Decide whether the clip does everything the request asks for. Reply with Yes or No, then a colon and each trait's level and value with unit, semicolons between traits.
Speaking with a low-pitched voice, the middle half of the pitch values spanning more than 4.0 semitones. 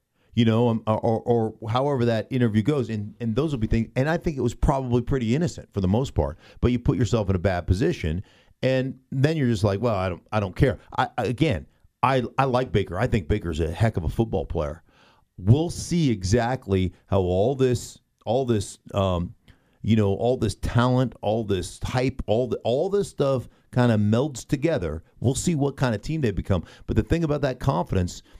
Yes: low, 115 Hz; average, 4.4 semitones